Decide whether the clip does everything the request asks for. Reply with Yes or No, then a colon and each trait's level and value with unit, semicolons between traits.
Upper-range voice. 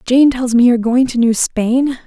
Yes: high, 245 Hz